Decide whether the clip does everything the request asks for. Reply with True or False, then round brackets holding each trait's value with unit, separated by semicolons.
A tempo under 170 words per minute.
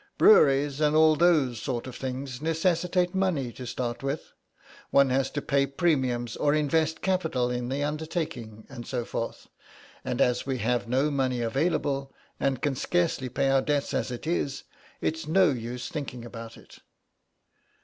True (160 wpm)